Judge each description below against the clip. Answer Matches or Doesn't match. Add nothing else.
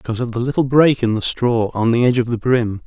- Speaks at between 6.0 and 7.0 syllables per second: Matches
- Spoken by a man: Matches